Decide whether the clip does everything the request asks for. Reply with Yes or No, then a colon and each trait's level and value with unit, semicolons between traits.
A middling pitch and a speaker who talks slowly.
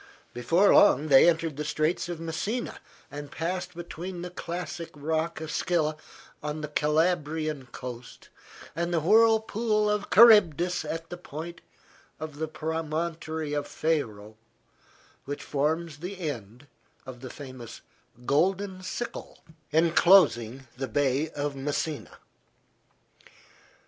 Yes: medium, 160 Hz; slow, 120 wpm